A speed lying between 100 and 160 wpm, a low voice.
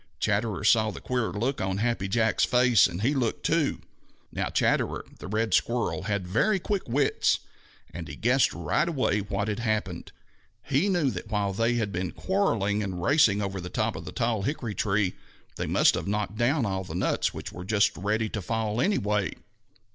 No: average, 190 wpm; low, 110 Hz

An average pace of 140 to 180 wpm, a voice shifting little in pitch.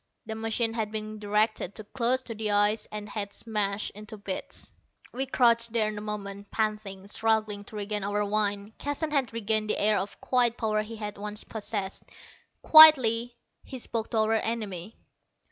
Yes: average, 170 wpm; narrow, 1.7 semitones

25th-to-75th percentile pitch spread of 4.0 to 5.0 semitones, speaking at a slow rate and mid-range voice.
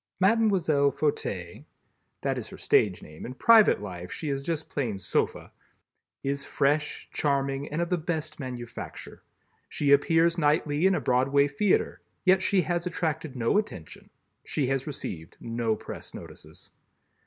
No: average, 4.7 semitones; average, 145 wpm; medium, 145 Hz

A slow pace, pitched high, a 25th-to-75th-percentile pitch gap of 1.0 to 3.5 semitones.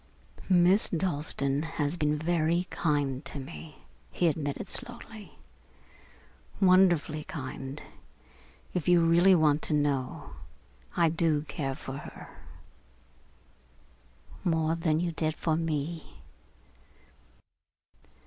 No: slow, 100 wpm; medium, 160 Hz; average, 2.8 semitones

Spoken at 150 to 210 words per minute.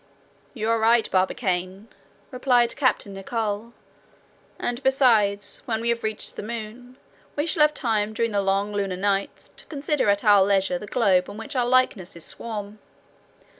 Yes: average, 160 wpm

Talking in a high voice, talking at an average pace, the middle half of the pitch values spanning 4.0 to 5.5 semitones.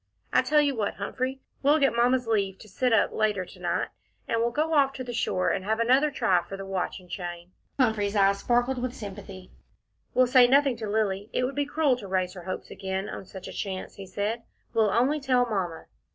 No: high, 220 Hz; fast, 225 wpm; average, 4.8 semitones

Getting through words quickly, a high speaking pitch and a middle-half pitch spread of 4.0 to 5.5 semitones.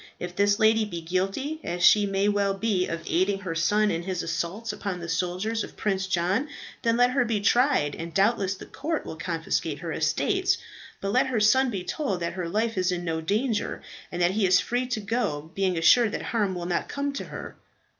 Yes: fast, 215 wpm; high, 195 Hz; average, 4.4 semitones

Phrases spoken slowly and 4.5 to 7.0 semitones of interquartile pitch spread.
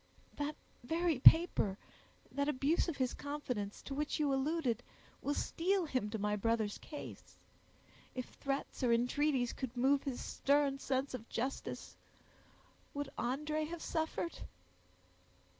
No: slow, 130 wpm; average, 3.5 semitones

